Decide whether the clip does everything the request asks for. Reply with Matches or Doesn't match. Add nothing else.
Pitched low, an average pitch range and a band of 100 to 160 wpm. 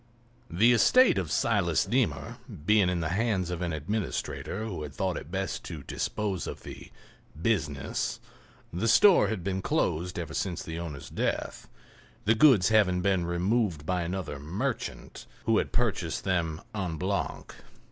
Matches